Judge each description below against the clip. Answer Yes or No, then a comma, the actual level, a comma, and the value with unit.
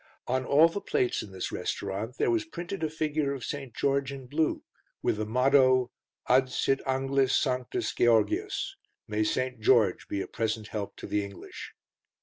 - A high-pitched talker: No, low, 130 Hz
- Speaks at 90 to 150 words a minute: No, average, 165 wpm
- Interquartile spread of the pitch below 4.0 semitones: No, average, 4.5 semitones